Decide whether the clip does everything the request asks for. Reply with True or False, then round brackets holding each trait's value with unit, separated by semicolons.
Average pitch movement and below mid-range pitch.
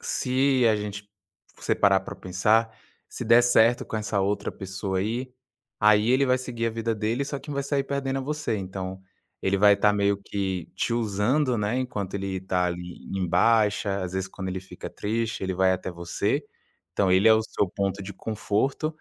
True (3.8 semitones; 105 Hz)